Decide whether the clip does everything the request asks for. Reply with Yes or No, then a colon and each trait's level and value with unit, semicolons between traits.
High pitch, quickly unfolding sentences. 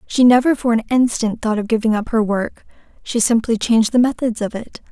Yes: high, 230 Hz; fast, 220 wpm